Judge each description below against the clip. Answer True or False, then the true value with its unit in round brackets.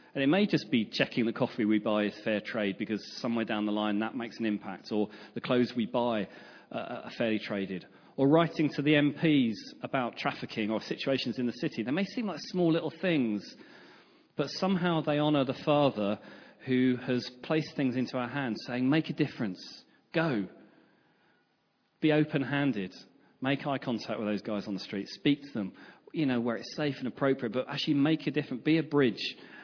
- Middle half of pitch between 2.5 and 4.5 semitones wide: False (5.4 semitones)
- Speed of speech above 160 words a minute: True (195 wpm)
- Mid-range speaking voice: False (125 Hz)